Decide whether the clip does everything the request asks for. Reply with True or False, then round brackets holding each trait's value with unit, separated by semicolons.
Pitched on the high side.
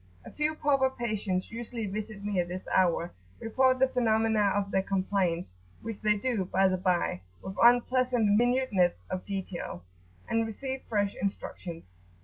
True (210 Hz)